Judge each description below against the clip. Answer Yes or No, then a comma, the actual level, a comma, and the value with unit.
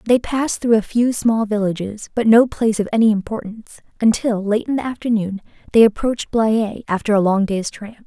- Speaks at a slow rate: No, average, 195 wpm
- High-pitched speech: Yes, high, 220 Hz